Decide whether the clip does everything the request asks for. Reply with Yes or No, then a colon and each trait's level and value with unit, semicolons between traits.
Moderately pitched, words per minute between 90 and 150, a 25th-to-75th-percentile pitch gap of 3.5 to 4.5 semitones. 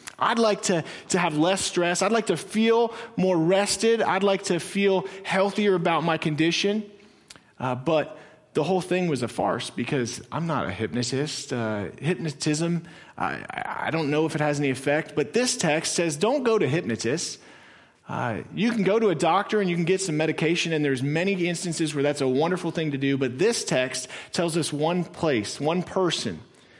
No: medium, 170 Hz; average, 195 wpm; average, 4.2 semitones